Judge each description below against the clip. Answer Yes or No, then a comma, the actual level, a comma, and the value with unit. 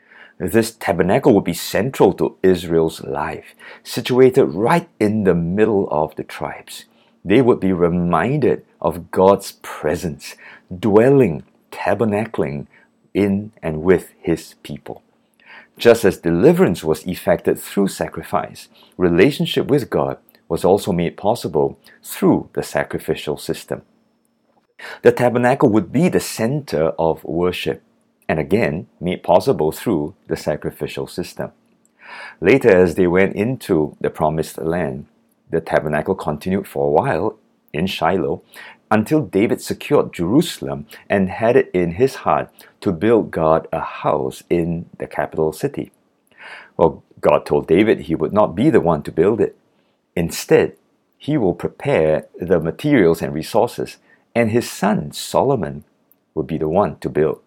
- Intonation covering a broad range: Yes, wide, 5.7 semitones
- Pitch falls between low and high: No, very low, 95 Hz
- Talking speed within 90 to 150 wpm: Yes, slow, 135 wpm